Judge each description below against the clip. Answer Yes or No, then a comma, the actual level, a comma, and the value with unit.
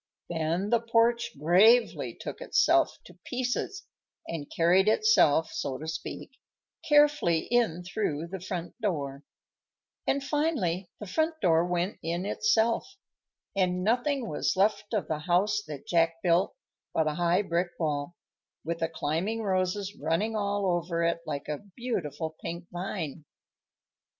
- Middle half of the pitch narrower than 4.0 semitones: No, average, 5.1 semitones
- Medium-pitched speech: Yes, medium, 180 Hz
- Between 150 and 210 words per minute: No, average, 140 wpm